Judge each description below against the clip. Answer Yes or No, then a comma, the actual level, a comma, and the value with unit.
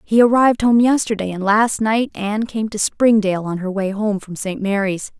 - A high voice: Yes, high, 210 Hz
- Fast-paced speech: Yes, fast, 210 wpm